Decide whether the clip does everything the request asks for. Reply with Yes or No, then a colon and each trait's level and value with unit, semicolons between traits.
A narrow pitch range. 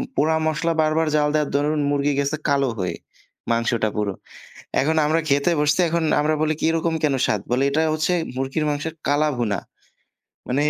Yes: narrow, 2.3 semitones